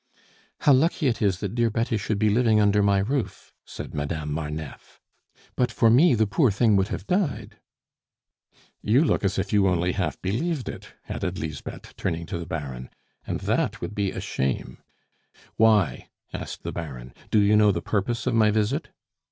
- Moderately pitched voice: No, low, 105 Hz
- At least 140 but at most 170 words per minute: No, average, 185 wpm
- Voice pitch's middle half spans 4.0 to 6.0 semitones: Yes, average, 4.8 semitones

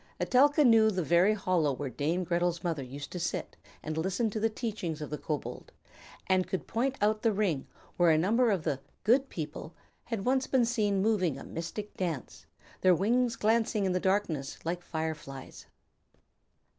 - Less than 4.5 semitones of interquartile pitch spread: No, wide, 5.4 semitones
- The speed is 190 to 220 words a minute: No, average, 180 wpm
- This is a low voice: No, medium, 185 Hz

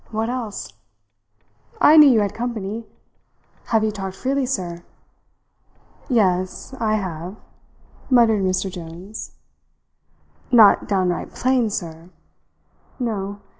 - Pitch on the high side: Yes, high, 210 Hz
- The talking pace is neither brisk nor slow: No, slow, 100 wpm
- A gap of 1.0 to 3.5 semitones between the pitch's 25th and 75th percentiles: No, average, 4.0 semitones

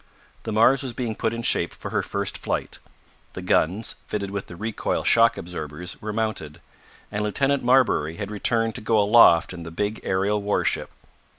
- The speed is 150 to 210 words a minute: Yes, average, 180 wpm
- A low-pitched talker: Yes, low, 105 Hz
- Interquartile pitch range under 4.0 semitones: Yes, average, 3.4 semitones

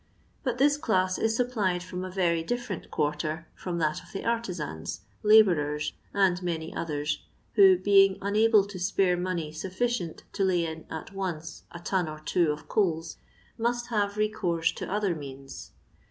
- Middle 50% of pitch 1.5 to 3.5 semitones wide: No, average, 4.0 semitones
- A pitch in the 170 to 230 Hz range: Yes, medium, 185 Hz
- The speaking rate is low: No, average, 165 wpm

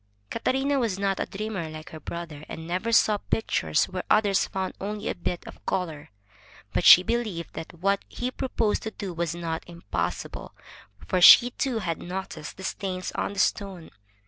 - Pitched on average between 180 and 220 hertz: Yes, high, 190 Hz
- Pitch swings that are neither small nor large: Yes, average, 3.9 semitones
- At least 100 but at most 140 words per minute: No, average, 175 wpm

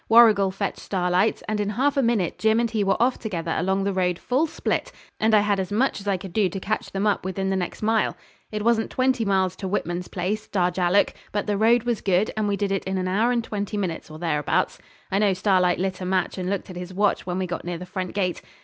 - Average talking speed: No, fast, 255 wpm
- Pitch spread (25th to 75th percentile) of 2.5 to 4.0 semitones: Yes, average, 2.8 semitones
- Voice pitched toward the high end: Yes, high, 195 Hz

